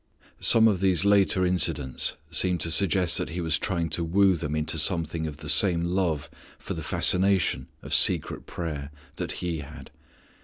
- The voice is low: Yes, very low, 85 Hz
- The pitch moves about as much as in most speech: Yes, average, 3.0 semitones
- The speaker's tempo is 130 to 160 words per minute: No, average, 170 wpm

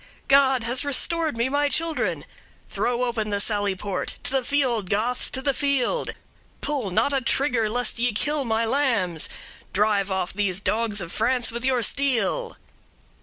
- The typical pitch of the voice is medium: No, high, 240 Hz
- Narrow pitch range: No, average, 4.7 semitones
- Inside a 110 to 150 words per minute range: No, average, 165 wpm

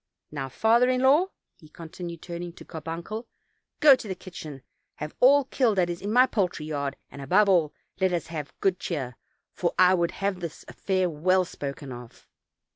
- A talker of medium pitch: Yes, medium, 175 Hz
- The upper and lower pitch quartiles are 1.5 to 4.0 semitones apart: No, average, 4.7 semitones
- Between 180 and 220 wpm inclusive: Yes, average, 185 wpm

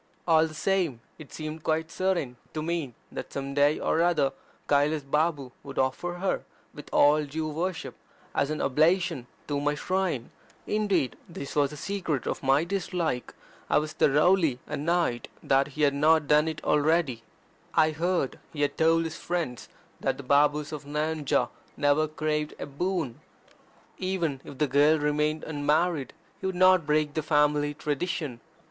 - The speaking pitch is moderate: Yes, medium, 150 Hz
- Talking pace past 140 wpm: Yes, average, 160 wpm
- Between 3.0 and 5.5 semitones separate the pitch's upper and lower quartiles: No, narrow, 2.5 semitones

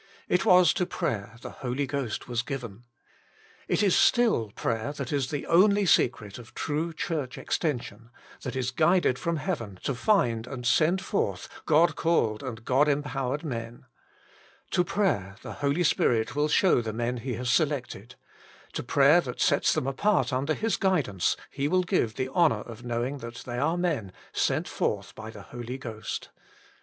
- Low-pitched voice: Yes, low, 130 Hz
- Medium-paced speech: Yes, average, 170 wpm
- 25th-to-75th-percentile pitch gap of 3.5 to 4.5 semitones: No, wide, 5.6 semitones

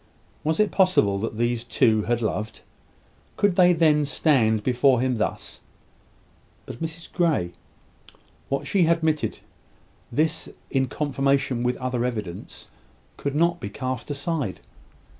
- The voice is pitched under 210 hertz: Yes, low, 135 Hz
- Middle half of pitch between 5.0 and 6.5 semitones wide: Yes, average, 5.3 semitones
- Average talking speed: No, slow, 125 wpm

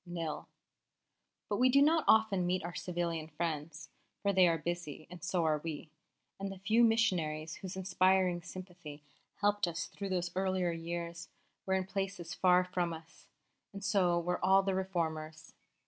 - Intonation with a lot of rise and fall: No, narrow, 2.5 semitones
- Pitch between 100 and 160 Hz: No, medium, 180 Hz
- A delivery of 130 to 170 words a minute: Yes, average, 165 wpm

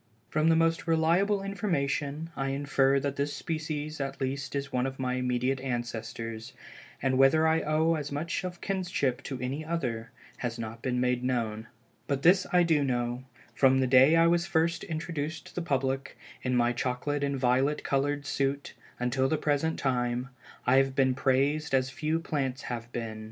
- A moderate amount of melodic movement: Yes, average, 3.7 semitones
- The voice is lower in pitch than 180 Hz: Yes, low, 135 Hz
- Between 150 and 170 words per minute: No, average, 180 wpm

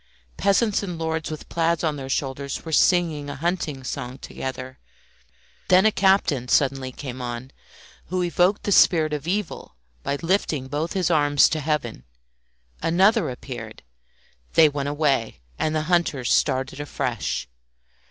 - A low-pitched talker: No, medium, 150 Hz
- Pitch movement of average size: Yes, average, 4.6 semitones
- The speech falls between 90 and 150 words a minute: Yes, average, 145 wpm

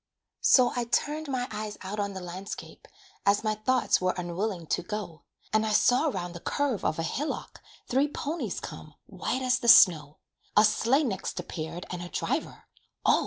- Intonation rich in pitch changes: Yes, wide, 5.9 semitones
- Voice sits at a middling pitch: No, high, 210 Hz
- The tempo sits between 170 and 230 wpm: Yes, average, 180 wpm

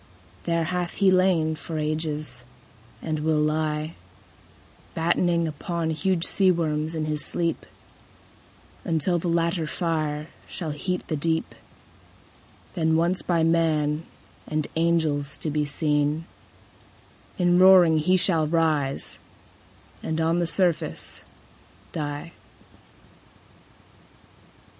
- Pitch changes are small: Yes, narrow, 1.9 semitones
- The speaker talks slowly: Yes, slow, 105 wpm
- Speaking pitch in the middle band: Yes, medium, 160 Hz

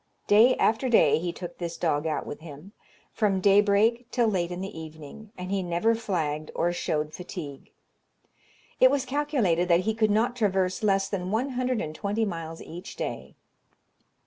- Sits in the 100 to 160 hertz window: No, high, 195 Hz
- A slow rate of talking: No, average, 175 wpm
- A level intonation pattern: No, average, 4.6 semitones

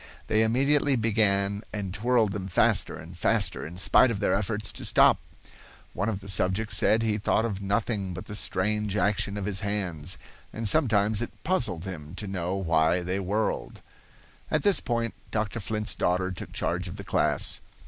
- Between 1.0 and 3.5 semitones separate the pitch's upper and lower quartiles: Yes, average, 2.9 semitones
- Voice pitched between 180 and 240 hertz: No, low, 100 Hz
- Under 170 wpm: No, average, 180 wpm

